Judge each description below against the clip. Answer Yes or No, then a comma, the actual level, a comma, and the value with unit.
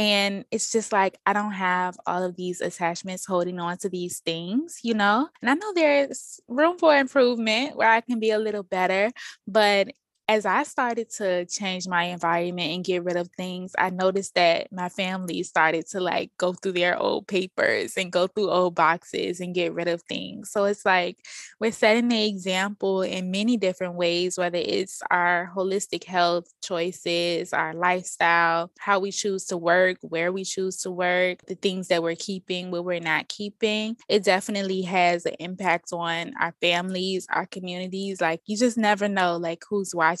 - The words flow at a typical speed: Yes, average, 185 wpm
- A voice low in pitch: No, medium, 185 Hz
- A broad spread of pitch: No, average, 2.8 semitones